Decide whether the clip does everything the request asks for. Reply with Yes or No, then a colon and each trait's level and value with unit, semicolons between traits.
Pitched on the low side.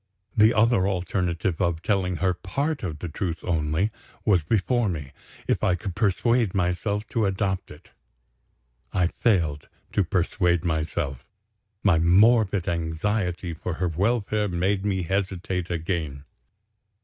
Yes: very low, 90 Hz